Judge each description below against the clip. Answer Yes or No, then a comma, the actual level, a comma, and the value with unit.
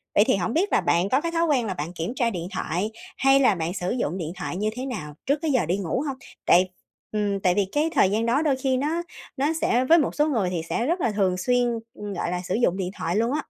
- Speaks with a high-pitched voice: Yes, high, 220 Hz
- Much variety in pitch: Yes, wide, 6.8 semitones